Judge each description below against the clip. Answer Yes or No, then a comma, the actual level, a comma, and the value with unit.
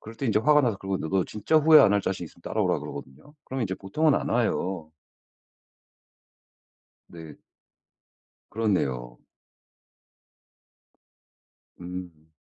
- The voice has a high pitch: No, very low, 95 Hz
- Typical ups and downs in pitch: No, wide, 5.7 semitones